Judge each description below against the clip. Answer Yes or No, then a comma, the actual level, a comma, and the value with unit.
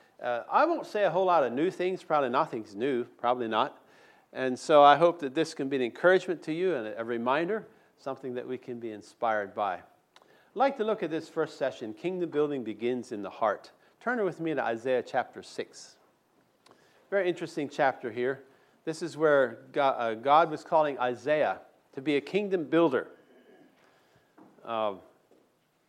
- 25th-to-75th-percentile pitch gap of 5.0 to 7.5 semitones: Yes, wide, 5.5 semitones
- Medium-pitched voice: Yes, medium, 155 Hz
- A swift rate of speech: No, average, 175 wpm